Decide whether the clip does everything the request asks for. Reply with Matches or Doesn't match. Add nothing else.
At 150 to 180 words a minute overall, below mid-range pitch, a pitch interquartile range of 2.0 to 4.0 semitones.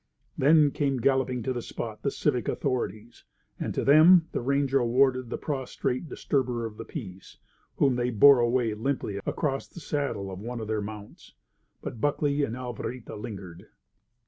Matches